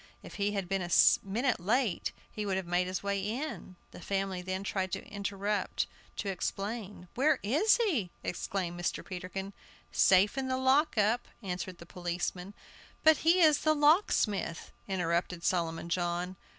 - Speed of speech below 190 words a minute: Yes, average, 160 wpm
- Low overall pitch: No, high, 195 Hz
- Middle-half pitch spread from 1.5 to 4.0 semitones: No, average, 4.9 semitones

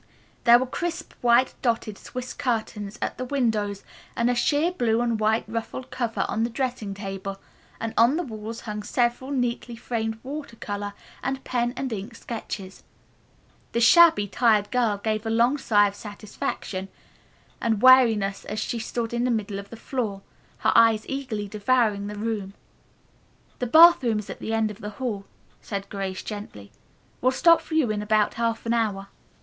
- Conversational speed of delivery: Yes, average, 175 wpm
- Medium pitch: No, high, 225 Hz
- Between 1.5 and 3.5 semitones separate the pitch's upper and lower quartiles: Yes, average, 3.0 semitones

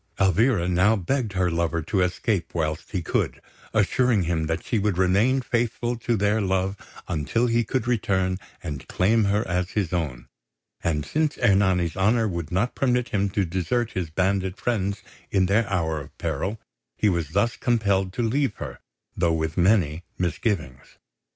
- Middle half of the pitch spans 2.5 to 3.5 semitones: No, average, 4.4 semitones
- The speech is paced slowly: No, average, 165 wpm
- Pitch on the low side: Yes, very low, 95 Hz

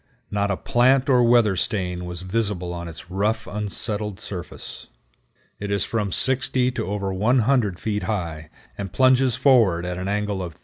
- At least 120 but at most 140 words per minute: No, average, 170 wpm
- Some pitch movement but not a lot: Yes, average, 4.4 semitones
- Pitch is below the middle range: Yes, low, 105 Hz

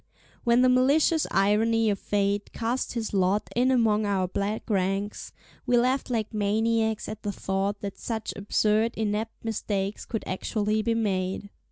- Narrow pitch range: Yes, narrow, 2.2 semitones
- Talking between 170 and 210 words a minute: No, average, 155 wpm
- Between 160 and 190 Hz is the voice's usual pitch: No, high, 215 Hz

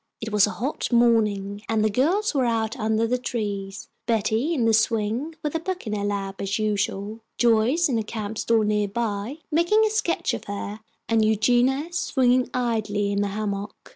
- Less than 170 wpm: No, average, 190 wpm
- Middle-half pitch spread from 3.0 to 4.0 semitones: Yes, average, 3.5 semitones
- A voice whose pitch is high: Yes, high, 220 Hz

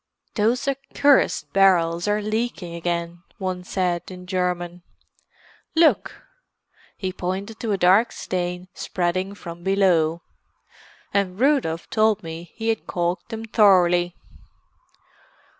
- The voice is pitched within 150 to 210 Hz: Yes, medium, 185 Hz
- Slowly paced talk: Yes, slow, 110 wpm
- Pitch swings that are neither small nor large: Yes, average, 3.4 semitones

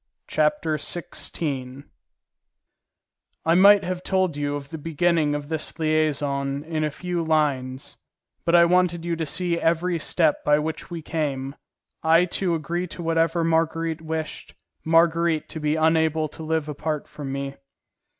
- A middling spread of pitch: No, narrow, 2.1 semitones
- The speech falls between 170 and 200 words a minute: No, average, 150 wpm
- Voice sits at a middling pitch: Yes, medium, 160 Hz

